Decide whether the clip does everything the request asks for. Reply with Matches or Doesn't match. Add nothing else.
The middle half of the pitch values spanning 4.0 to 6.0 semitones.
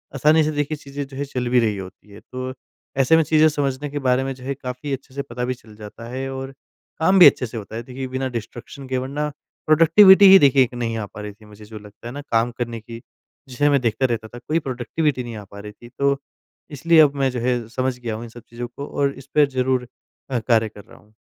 Doesn't match